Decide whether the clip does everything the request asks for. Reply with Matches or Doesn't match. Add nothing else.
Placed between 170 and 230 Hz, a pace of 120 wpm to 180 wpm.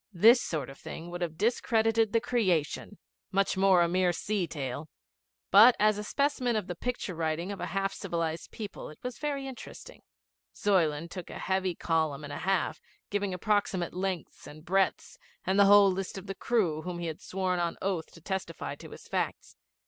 Doesn't match